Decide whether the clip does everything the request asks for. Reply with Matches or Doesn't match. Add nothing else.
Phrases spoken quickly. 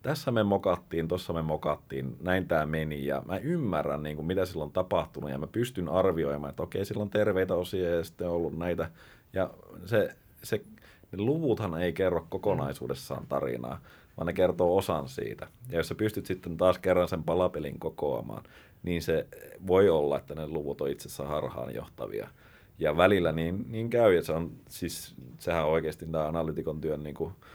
Matches